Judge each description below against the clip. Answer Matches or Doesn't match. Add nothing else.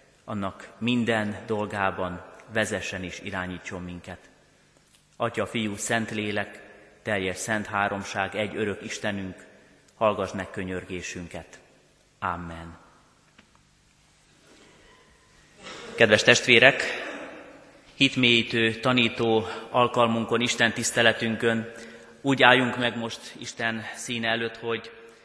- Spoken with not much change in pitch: Doesn't match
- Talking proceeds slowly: Matches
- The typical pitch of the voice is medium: Doesn't match